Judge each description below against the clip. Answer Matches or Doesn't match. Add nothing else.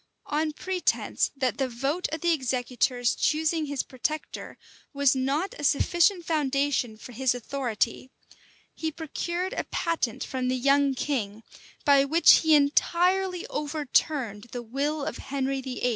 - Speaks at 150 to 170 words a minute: Doesn't match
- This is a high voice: Matches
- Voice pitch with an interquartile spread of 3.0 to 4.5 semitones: Matches